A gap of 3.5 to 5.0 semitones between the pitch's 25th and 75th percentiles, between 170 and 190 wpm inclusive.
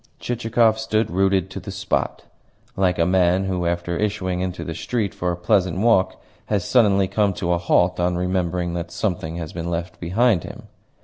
No: narrow, 2.5 semitones; average, 185 wpm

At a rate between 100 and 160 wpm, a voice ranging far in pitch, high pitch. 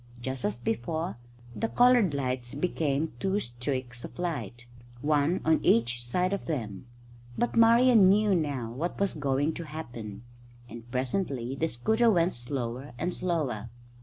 No: average, 145 wpm; wide, 6.7 semitones; medium, 145 Hz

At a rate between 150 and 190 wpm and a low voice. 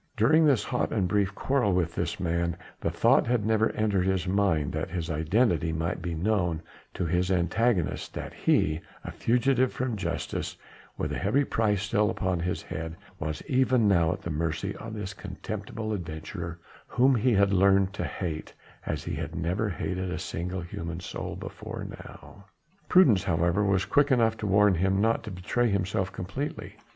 Yes: average, 180 wpm; very low, 95 Hz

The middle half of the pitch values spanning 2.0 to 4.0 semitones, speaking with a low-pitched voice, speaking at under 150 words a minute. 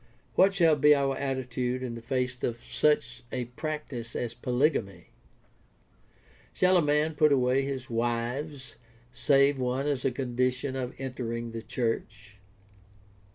Yes: average, 2.9 semitones; low, 130 Hz; average, 140 wpm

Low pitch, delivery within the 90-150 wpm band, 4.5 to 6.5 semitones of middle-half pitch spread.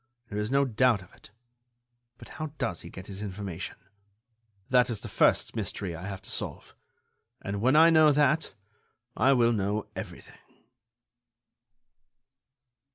Yes: low, 105 Hz; average, 145 wpm; wide, 5.6 semitones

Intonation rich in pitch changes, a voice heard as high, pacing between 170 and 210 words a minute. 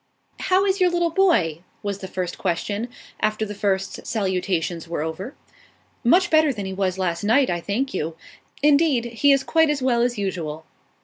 Yes: wide, 7.6 semitones; high, 205 Hz; average, 180 wpm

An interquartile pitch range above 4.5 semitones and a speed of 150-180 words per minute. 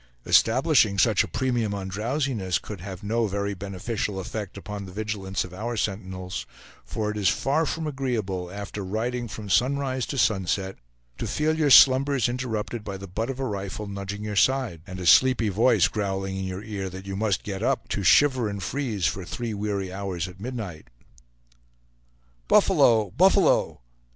No: average, 4.0 semitones; average, 170 wpm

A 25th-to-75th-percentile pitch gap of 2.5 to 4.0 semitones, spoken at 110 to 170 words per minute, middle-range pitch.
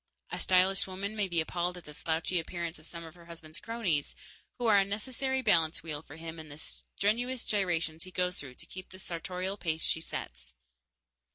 No: average, 3.5 semitones; average, 200 wpm; medium, 175 Hz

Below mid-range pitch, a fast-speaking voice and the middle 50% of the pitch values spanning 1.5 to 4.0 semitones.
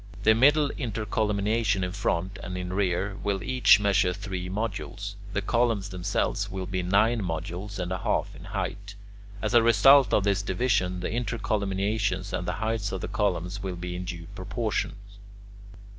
No: low, 100 Hz; average, 170 wpm; average, 2.9 semitones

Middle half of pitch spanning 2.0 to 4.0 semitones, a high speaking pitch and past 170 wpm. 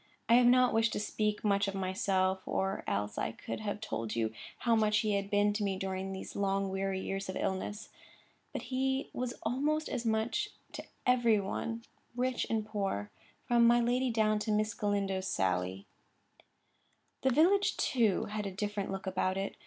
Yes: average, 3.3 semitones; high, 210 Hz; average, 180 wpm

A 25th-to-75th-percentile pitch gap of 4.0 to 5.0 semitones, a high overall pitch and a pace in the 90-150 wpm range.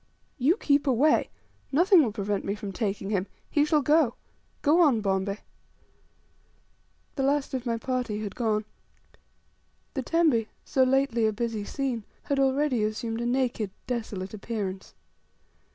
Yes: average, 4.5 semitones; high, 240 Hz; average, 140 wpm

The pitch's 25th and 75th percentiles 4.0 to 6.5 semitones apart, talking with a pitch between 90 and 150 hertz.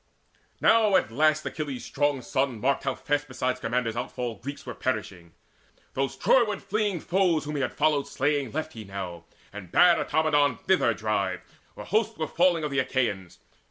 Yes: average, 5.2 semitones; medium, 140 Hz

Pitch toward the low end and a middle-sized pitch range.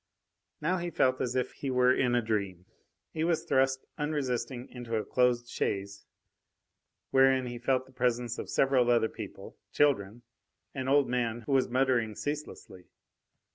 No: low, 125 Hz; narrow, 2.1 semitones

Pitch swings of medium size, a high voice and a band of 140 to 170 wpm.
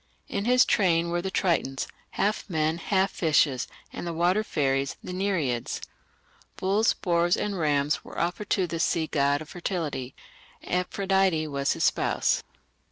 No: average, 4.3 semitones; medium, 170 Hz; average, 150 wpm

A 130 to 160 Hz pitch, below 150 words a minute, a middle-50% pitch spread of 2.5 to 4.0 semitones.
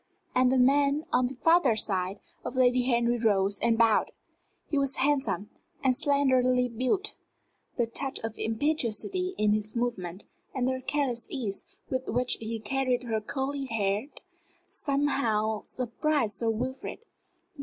No: very high, 250 Hz; average, 140 wpm; average, 3.6 semitones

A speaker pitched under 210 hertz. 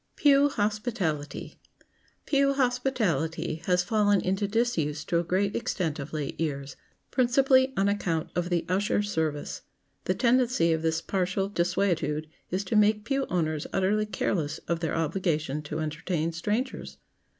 Yes: medium, 185 Hz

